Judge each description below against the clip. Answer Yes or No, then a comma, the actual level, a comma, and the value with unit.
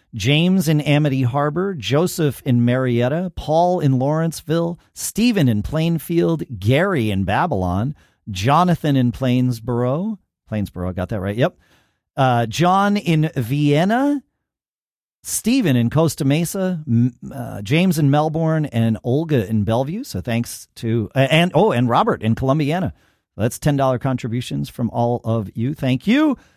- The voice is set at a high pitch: No, low, 135 Hz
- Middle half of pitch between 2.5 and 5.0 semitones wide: No, wide, 5.6 semitones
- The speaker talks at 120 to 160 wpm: Yes, average, 140 wpm